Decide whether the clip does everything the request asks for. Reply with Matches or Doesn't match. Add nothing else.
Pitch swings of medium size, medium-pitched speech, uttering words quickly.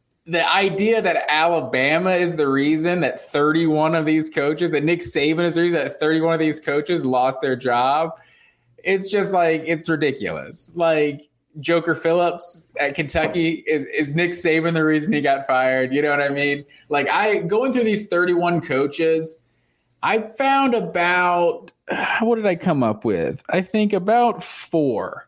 Doesn't match